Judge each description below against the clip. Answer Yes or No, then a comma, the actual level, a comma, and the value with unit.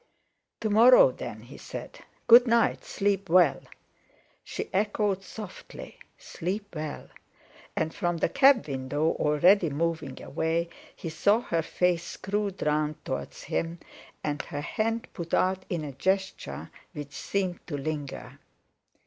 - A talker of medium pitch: Yes, medium, 175 Hz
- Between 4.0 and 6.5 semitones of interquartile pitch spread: Yes, average, 4.9 semitones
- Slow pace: Yes, slow, 130 wpm